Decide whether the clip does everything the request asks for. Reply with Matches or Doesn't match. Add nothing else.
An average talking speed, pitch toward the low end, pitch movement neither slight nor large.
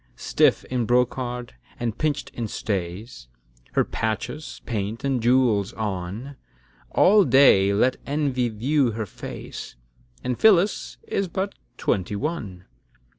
Doesn't match